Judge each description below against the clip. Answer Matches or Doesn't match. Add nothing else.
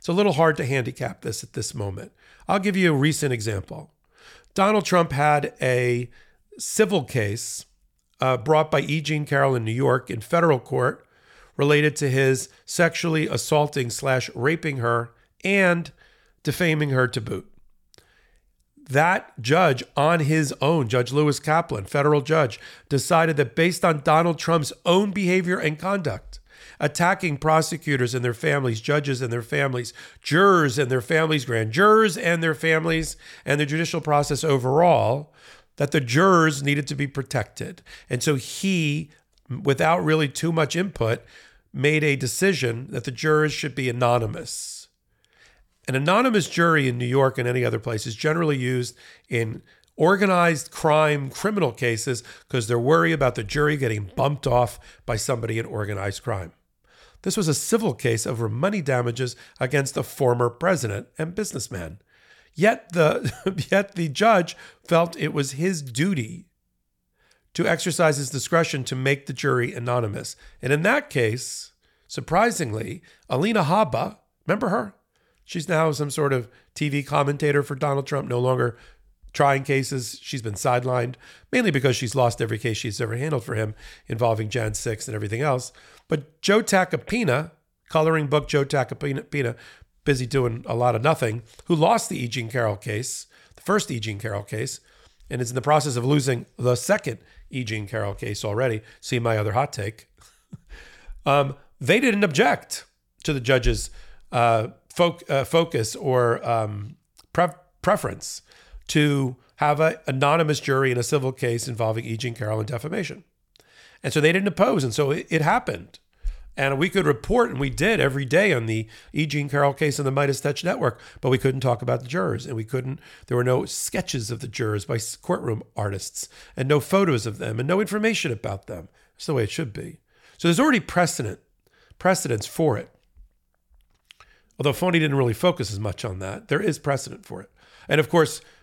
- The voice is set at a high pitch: Doesn't match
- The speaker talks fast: Doesn't match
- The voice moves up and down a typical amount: Matches